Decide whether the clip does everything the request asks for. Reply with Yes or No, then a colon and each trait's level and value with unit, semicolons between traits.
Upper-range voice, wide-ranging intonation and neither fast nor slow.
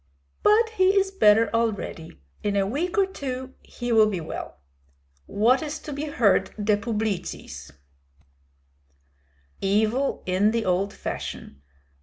No: high, 225 Hz; wide, 5.9 semitones; slow, 130 wpm